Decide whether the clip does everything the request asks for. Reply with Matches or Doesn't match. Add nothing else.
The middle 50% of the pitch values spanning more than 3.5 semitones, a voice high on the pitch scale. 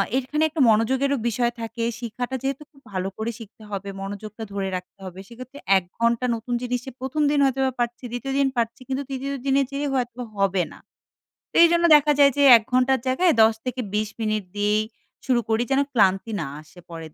Matches